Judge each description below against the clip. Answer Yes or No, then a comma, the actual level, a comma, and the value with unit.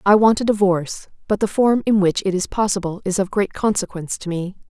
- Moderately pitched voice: No, high, 195 Hz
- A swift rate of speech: Yes, fast, 230 wpm